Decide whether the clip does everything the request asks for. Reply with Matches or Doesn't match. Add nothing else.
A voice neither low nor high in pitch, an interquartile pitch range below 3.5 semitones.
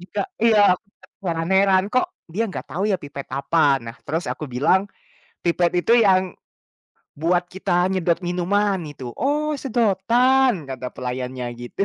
Doesn't match